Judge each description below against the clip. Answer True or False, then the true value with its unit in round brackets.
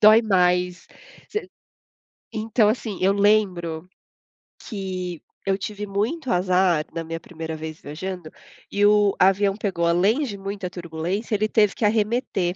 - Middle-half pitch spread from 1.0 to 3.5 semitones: True (3.0 semitones)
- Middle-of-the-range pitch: False (195 Hz)